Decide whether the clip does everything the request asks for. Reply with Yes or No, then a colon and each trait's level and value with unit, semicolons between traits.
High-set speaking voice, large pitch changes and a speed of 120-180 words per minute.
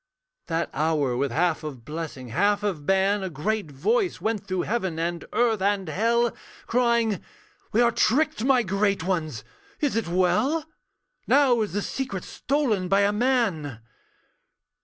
Yes: high, 200 Hz; wide, 6.1 semitones; average, 150 wpm